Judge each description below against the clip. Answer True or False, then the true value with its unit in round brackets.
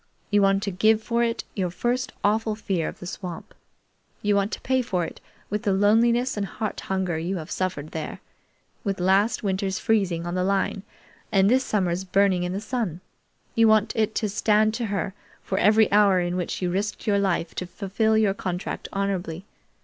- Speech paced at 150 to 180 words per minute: False (195 wpm)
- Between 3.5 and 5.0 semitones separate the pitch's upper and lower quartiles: False (2.9 semitones)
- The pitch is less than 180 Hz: False (200 Hz)